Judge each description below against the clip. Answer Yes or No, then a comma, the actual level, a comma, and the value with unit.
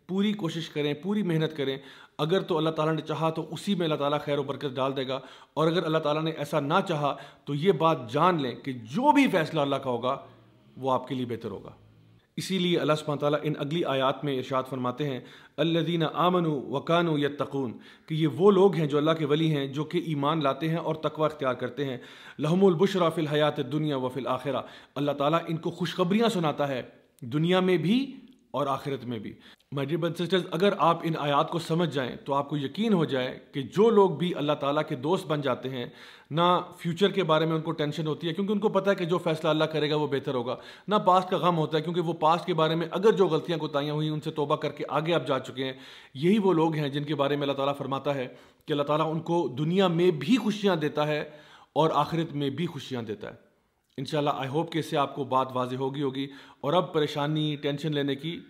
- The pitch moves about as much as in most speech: Yes, average, 3.4 semitones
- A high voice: No, medium, 155 Hz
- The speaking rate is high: Yes, fast, 235 wpm